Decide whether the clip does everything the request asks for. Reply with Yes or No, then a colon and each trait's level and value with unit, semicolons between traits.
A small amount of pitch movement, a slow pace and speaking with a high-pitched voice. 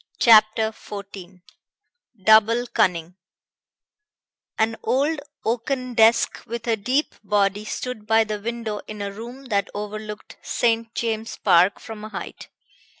Yes: narrow, 2.0 semitones; slow, 125 wpm; high, 220 Hz